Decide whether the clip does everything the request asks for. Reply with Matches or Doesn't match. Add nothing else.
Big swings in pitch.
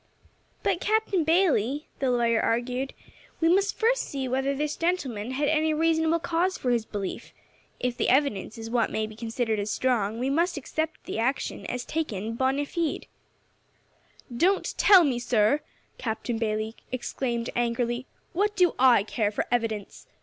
Matches